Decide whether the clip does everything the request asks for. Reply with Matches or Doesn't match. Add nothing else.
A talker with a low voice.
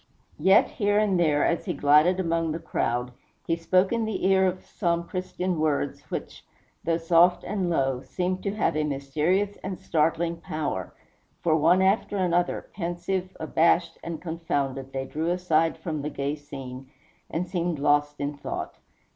Doesn't match